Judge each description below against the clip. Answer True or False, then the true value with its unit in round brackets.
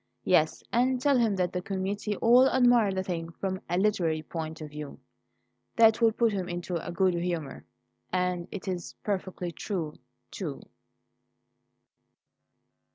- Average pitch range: True (4.0 semitones)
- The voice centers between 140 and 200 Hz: True (185 Hz)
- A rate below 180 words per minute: True (140 wpm)